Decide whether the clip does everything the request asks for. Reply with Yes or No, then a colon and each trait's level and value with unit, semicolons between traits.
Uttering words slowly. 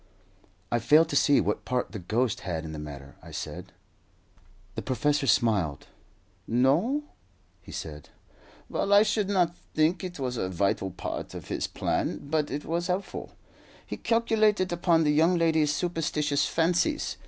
No: average, 155 wpm